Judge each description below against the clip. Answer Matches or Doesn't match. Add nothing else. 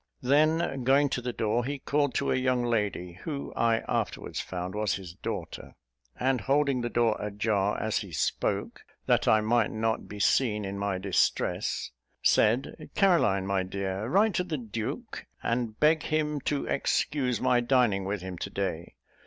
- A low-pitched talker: Matches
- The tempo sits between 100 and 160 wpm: Doesn't match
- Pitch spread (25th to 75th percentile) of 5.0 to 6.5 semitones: Matches